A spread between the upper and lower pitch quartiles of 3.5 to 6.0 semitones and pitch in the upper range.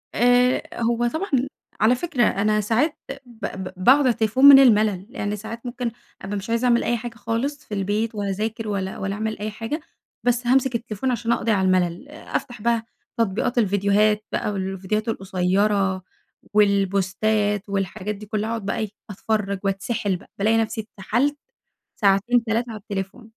No: average, 3.1 semitones; high, 215 Hz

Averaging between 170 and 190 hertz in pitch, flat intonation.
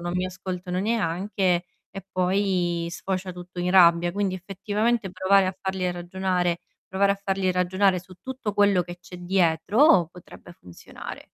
Yes: medium, 185 Hz; narrow, 1.8 semitones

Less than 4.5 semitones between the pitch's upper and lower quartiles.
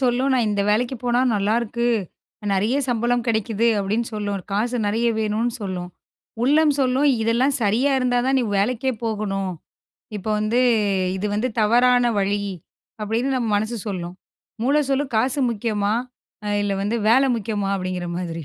Yes: average, 3.5 semitones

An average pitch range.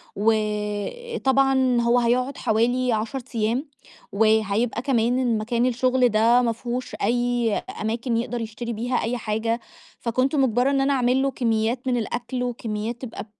No: narrow, 2.3 semitones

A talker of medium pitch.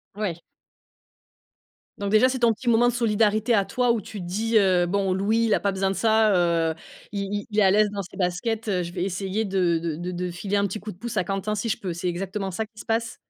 No: high, 200 Hz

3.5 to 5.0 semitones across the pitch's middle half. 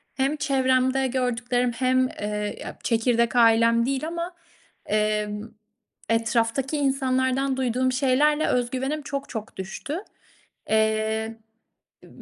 No: average, 2.9 semitones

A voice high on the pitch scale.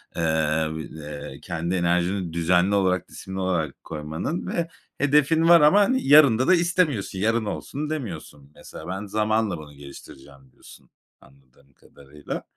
No: very low, 90 Hz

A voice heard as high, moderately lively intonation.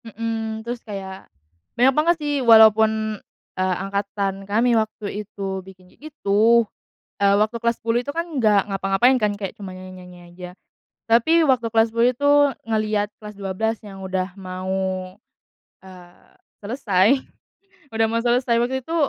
Yes: high, 215 Hz; average, 3.3 semitones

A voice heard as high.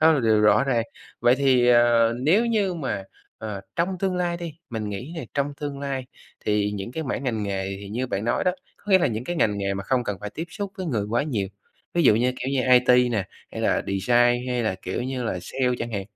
No: low, 125 Hz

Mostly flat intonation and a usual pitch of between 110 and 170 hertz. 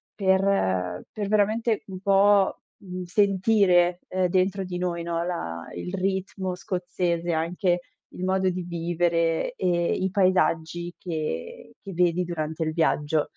No: narrow, 2.1 semitones; medium, 180 Hz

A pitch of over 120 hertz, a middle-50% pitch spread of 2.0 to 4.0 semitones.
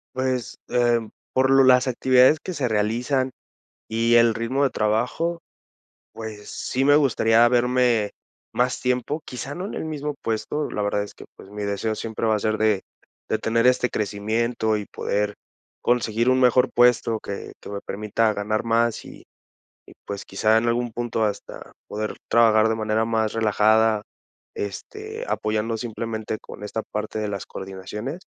No: low, 115 Hz; average, 2.7 semitones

